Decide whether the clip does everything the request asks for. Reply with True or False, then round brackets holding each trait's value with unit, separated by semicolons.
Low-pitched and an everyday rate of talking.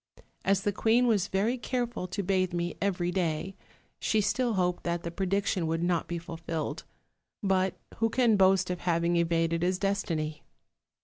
False (185 Hz; 165 wpm)